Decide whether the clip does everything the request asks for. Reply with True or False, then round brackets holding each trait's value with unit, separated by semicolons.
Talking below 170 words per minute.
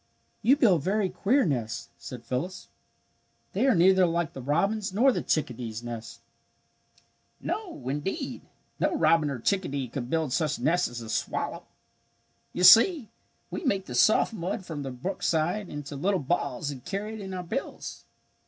True (160 wpm)